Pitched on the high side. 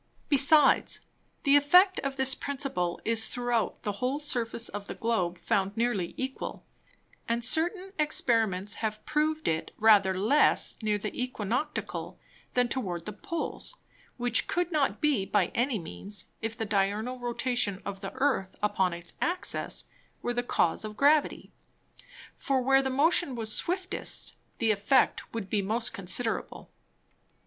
Yes: high, 235 Hz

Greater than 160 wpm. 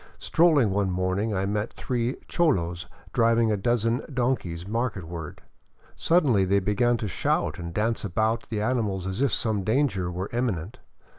No: average, 150 wpm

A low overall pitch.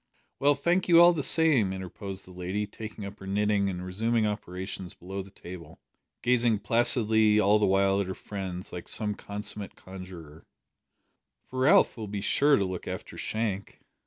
Yes: low, 100 Hz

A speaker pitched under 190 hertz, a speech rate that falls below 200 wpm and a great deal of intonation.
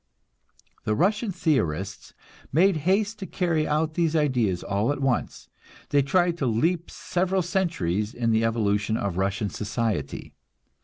Yes: medium, 140 Hz; average, 140 wpm; wide, 8.5 semitones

